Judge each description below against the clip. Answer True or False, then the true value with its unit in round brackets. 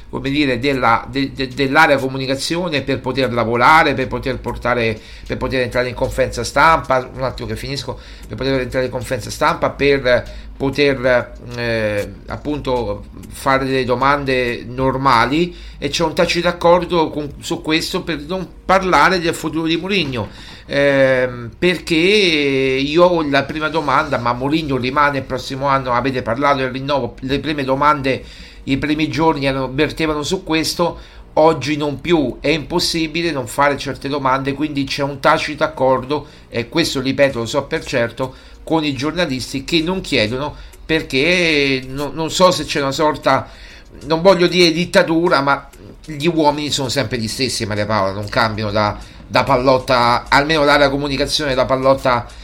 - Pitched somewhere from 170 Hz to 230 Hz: False (140 Hz)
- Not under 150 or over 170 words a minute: True (155 wpm)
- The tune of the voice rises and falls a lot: False (3.5 semitones)